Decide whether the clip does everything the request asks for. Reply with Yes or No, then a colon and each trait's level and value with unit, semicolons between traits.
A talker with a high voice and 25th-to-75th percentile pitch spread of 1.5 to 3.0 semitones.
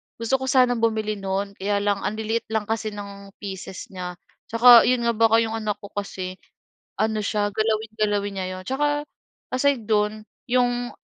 Yes: high, 215 Hz; narrow, 2.4 semitones